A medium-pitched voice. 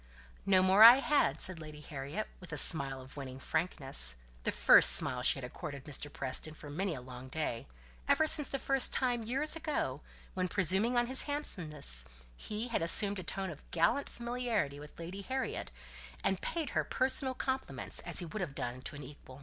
Yes: medium, 175 Hz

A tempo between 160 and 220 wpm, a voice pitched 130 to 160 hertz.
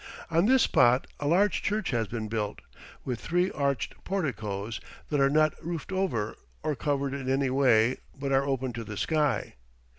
Yes: average, 175 wpm; medium, 140 Hz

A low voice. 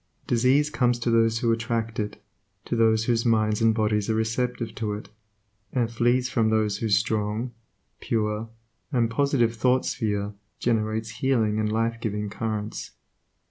Yes: low, 115 Hz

